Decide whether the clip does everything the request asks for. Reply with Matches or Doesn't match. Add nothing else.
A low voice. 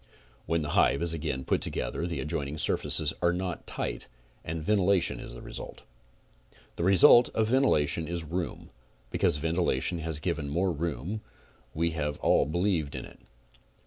Matches